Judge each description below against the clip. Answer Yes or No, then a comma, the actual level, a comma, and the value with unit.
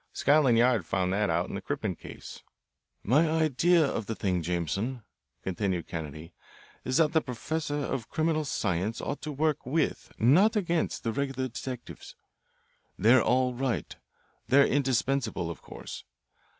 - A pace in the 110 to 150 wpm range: Yes, average, 145 wpm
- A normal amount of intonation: No, wide, 6.8 semitones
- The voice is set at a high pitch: No, low, 130 Hz